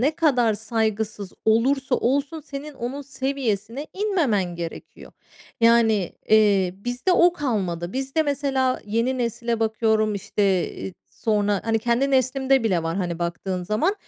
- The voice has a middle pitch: No, high, 230 Hz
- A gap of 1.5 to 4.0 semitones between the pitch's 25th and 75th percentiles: No, average, 4.7 semitones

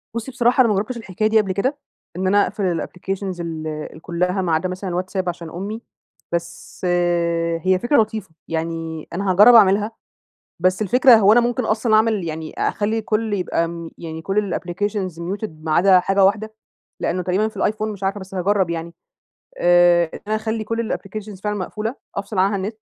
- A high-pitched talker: Yes, high, 195 Hz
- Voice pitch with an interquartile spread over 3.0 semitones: Yes, average, 3.6 semitones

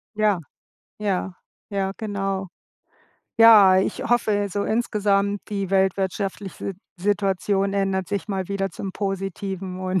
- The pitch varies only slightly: Yes, narrow, 1.2 semitones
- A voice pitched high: Yes, high, 195 Hz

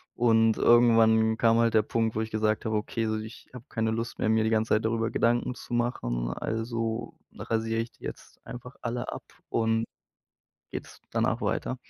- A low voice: Yes, low, 115 Hz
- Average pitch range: No, narrow, 0.9 semitones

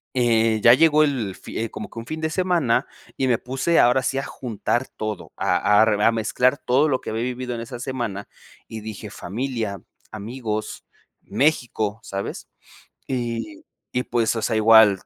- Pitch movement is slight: No, average, 3.2 semitones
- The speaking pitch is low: Yes, low, 120 Hz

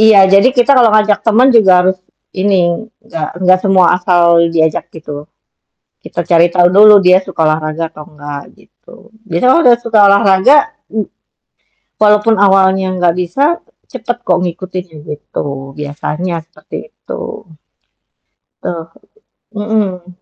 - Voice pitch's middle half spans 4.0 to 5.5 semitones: Yes, average, 4.3 semitones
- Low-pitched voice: No, high, 190 Hz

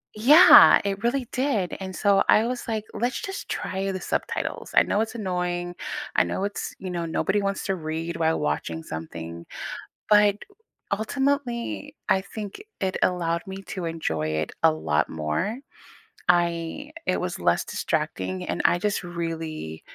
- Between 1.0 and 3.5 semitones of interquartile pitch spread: No, average, 4.6 semitones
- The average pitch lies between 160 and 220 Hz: Yes, medium, 185 Hz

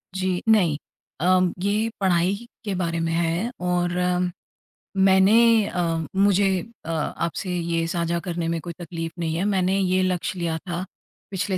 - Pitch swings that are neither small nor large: No, narrow, 2.2 semitones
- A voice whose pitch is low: No, medium, 180 Hz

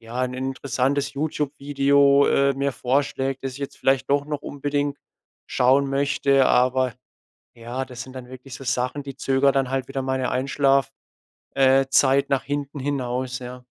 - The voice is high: No, low, 135 Hz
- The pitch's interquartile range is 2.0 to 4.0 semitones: No, narrow, 1.5 semitones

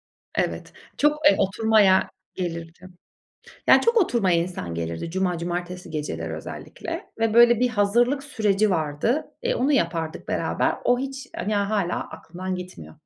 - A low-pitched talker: No, high, 190 Hz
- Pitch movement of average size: No, wide, 5.9 semitones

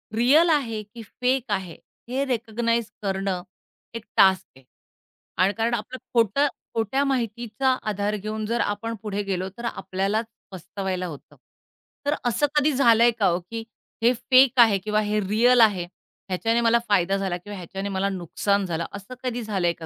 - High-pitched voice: Yes, high, 215 Hz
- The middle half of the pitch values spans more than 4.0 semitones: No, average, 3.6 semitones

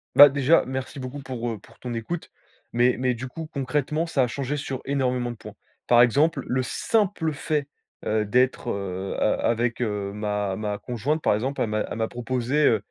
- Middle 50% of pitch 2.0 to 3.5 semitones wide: No, average, 4.0 semitones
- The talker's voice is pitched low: Yes, low, 125 Hz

